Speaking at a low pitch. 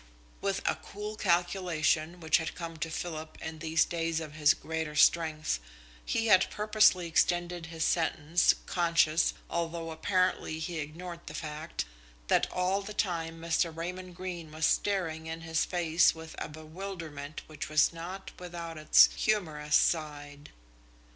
No: medium, 165 Hz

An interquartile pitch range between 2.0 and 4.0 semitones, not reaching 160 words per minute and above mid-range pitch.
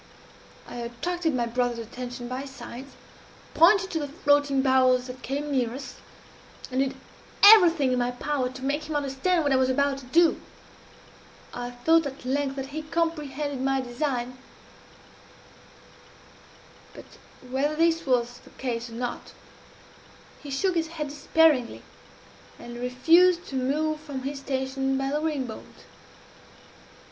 Yes: average, 3.3 semitones; average, 145 wpm; very high, 270 Hz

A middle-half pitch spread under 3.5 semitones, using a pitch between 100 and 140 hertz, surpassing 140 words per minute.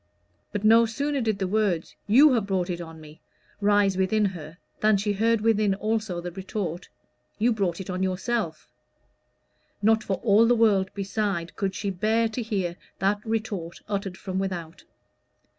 No: average, 2.9 semitones; high, 200 Hz; average, 165 wpm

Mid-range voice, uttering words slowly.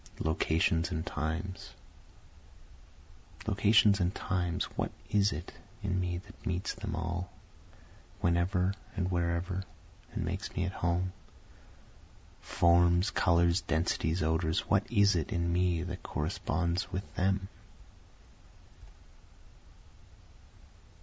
No: very low, 90 Hz; slow, 105 wpm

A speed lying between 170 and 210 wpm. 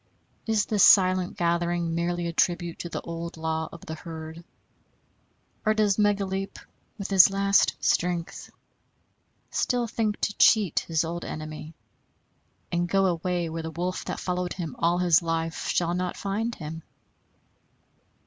No: average, 145 wpm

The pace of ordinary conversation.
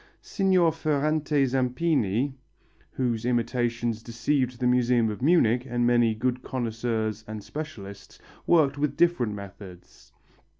No: slow, 115 wpm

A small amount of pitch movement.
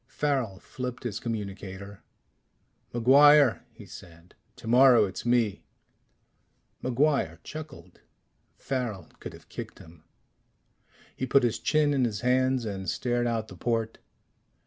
No: average, 4.5 semitones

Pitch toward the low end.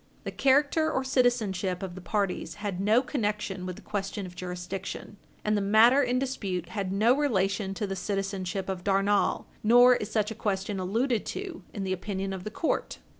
No: high, 205 Hz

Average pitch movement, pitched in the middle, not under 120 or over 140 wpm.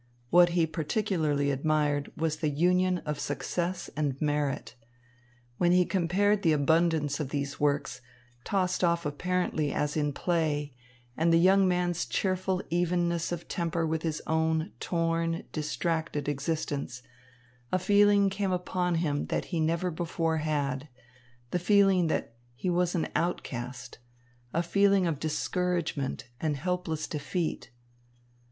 Yes: average, 3.3 semitones; medium, 165 Hz; slow, 135 wpm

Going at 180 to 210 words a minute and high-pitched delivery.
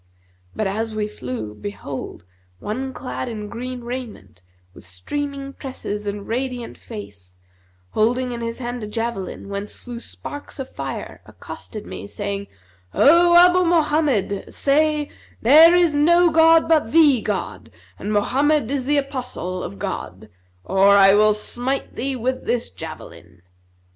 No: average, 140 wpm; high, 235 Hz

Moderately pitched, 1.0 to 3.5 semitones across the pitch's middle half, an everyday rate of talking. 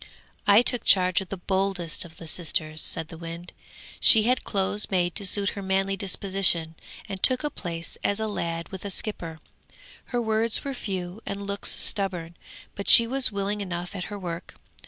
No: high, 195 Hz; average, 2.9 semitones; average, 185 wpm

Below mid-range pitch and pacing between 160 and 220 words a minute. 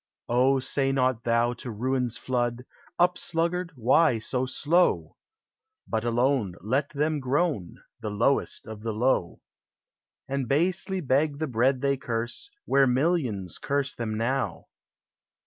No: low, 130 Hz; slow, 135 wpm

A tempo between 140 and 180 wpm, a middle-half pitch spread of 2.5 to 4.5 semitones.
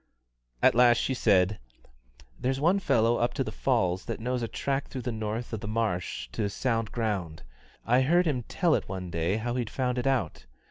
No: average, 200 wpm; average, 3.7 semitones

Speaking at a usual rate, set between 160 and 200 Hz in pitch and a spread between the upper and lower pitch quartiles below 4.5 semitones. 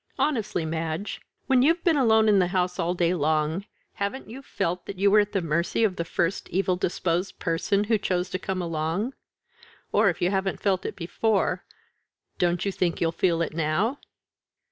Yes: average, 190 wpm; medium, 185 Hz; average, 3.6 semitones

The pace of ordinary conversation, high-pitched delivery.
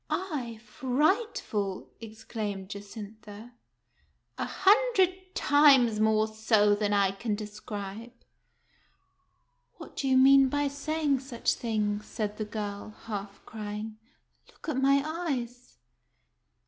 No: slow, 120 wpm; high, 225 Hz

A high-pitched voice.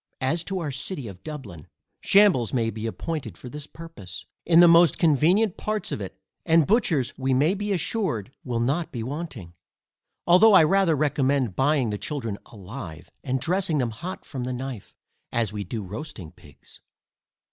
No: medium, 140 Hz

